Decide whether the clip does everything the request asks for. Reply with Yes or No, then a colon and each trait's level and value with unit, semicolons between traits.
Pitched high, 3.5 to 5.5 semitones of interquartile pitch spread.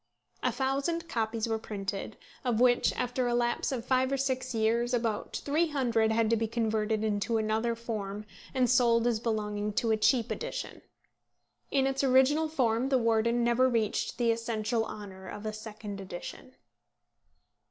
No: high, 230 Hz; average, 2.7 semitones